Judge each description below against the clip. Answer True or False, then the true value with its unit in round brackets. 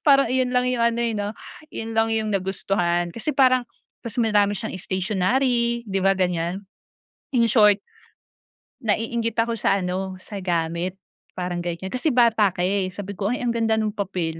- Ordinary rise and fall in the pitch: True (4.0 semitones)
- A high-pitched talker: True (210 Hz)